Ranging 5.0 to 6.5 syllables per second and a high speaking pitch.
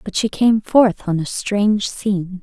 No: 4.3 syllables/s; high, 200 Hz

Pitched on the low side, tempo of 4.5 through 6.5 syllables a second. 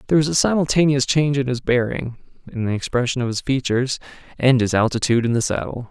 No: low, 130 Hz; 6.8 syllables/s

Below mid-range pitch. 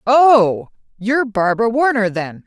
No: high, 225 Hz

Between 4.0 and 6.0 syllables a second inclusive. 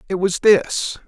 No: 3.8 syllables/s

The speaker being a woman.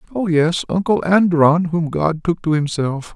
No: male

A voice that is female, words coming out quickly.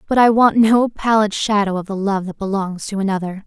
Yes: female; fast, 225 wpm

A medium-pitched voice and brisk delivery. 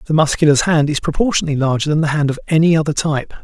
Yes: medium, 150 Hz; fast, 225 wpm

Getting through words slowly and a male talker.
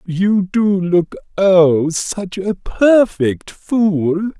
Yes: slow, 110 wpm; male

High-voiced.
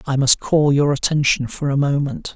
No: medium, 140 Hz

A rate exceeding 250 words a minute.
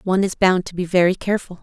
Yes: fast, 260 wpm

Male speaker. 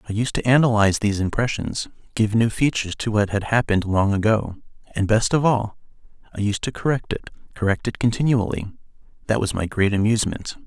Yes: male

